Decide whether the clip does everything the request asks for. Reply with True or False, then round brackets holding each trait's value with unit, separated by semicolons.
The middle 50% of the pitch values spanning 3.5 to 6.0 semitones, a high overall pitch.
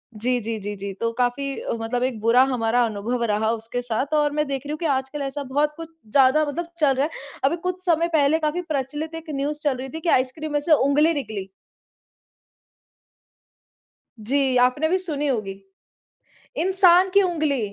True (4.0 semitones; 275 Hz)